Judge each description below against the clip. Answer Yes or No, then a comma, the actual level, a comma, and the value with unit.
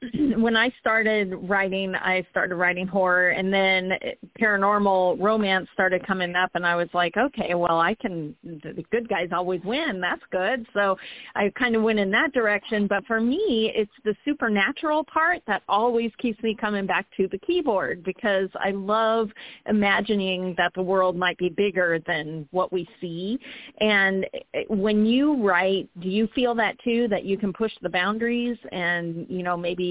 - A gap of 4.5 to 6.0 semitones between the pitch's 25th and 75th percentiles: No, average, 3.6 semitones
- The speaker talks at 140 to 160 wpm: No, average, 175 wpm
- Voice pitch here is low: No, high, 200 Hz